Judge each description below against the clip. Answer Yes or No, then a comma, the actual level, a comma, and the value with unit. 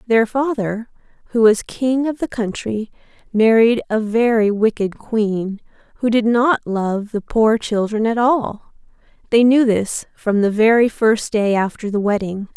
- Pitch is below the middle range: No, high, 220 Hz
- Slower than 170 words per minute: Yes, average, 160 wpm